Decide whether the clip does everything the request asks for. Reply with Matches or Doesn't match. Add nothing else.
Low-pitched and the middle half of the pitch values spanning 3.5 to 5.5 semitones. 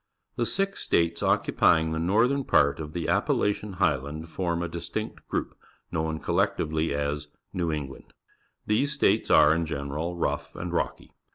Doesn't match